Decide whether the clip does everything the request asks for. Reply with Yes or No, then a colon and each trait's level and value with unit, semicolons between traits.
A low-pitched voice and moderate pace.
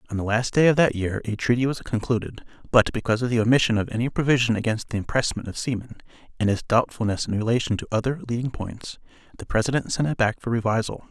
No: low, 115 Hz; fast, 215 wpm